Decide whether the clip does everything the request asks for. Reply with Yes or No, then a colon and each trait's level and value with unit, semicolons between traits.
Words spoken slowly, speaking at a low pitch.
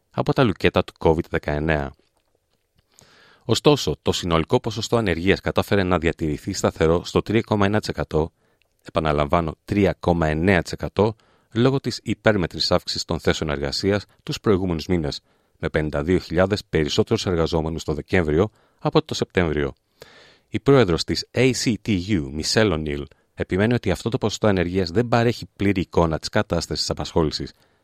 No: average, 125 wpm; very low, 90 Hz